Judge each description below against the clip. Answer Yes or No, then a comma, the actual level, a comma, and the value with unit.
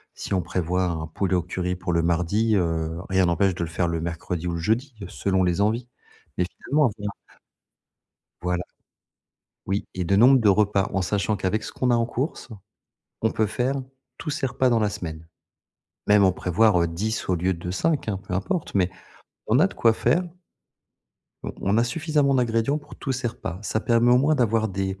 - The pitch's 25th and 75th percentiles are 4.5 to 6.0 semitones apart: Yes, average, 4.9 semitones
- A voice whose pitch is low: Yes, low, 100 Hz